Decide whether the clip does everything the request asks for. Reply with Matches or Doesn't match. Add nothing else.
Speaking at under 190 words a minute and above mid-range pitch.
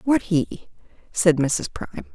Doesn't match